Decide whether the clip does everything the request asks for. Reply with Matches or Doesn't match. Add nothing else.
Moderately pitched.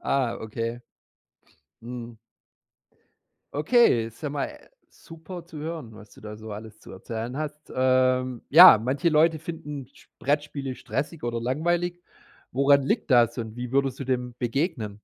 Doesn't match